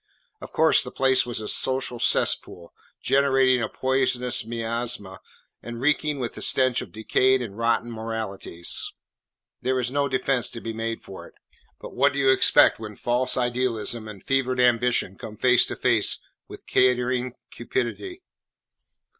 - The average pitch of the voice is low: Yes, low, 125 Hz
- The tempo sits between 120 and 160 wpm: Yes, average, 155 wpm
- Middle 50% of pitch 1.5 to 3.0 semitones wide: Yes, narrow, 2.4 semitones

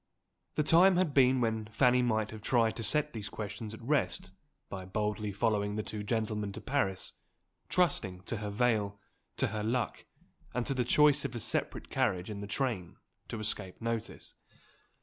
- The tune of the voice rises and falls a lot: No, average, 3.3 semitones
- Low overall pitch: Yes, low, 110 Hz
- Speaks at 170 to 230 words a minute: Yes, average, 175 wpm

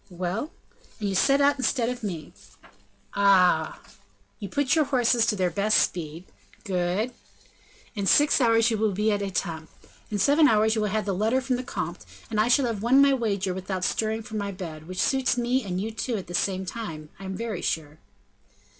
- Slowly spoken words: No, average, 200 wpm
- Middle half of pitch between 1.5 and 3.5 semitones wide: No, average, 4.5 semitones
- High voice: Yes, high, 210 Hz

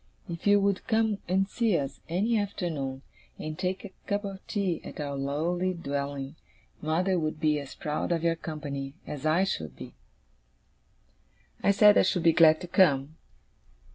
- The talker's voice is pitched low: No, medium, 165 Hz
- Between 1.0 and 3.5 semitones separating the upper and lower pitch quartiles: No, average, 4.6 semitones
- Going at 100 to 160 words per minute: No, average, 170 wpm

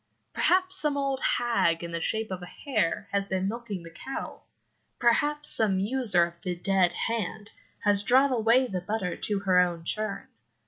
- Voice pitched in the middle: No, high, 205 Hz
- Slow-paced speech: No, average, 175 wpm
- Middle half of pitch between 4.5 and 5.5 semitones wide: Yes, average, 5.0 semitones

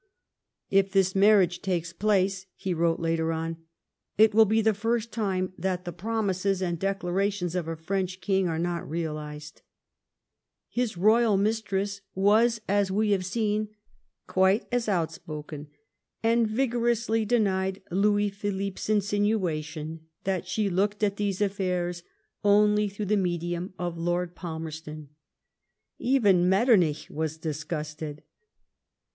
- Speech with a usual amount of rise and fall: Yes, average, 3.4 semitones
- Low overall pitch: No, high, 190 Hz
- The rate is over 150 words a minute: No, slow, 135 wpm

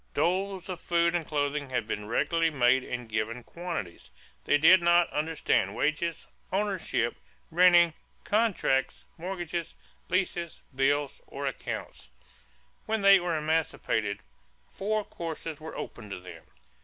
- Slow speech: Yes, slow, 125 wpm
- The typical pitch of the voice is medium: Yes, medium, 165 Hz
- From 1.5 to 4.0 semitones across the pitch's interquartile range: No, average, 4.8 semitones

